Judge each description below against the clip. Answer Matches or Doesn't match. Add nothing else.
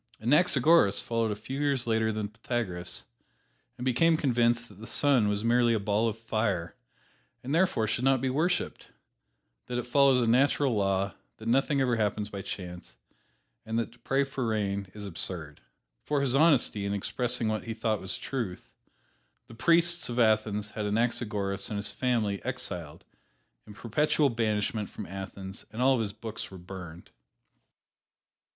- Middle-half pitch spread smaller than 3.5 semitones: Doesn't match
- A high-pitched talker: Doesn't match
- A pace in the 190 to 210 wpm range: Doesn't match